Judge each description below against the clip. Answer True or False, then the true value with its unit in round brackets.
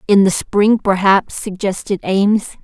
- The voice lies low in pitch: False (195 Hz)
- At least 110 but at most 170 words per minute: True (135 wpm)